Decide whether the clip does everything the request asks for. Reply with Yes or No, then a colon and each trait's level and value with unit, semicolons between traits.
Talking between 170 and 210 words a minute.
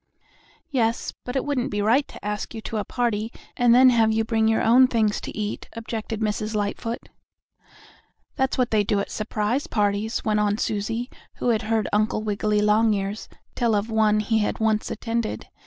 Yes: average, 180 wpm